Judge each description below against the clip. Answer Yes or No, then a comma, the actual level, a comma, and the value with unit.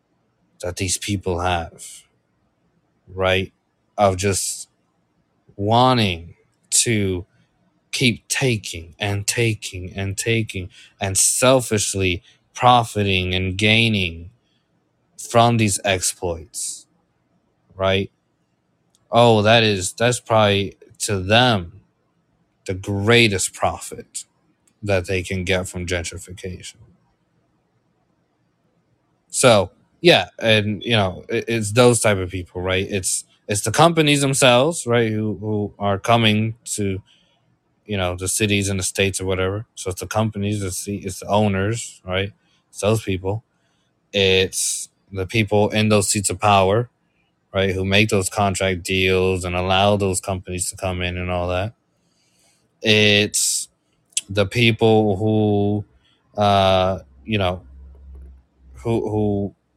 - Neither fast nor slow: No, slow, 115 wpm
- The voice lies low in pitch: Yes, low, 100 Hz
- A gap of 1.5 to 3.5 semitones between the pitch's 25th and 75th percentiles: Yes, average, 2.8 semitones